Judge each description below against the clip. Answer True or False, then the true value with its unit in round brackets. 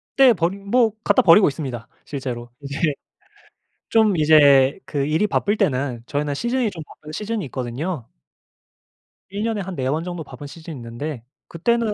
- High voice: False (155 Hz)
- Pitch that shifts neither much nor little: False (6.6 semitones)